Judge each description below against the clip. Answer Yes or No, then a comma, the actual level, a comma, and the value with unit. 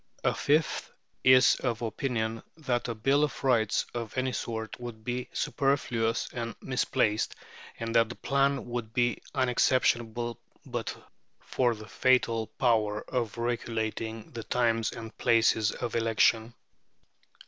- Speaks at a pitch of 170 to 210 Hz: No, low, 120 Hz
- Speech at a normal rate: No, slow, 130 wpm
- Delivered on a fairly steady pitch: Yes, narrow, 2.1 semitones